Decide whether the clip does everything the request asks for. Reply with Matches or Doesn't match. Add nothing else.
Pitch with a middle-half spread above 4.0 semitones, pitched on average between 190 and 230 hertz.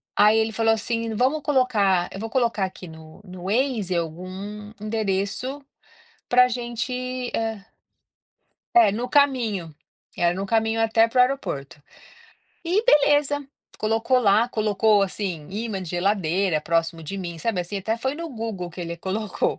Matches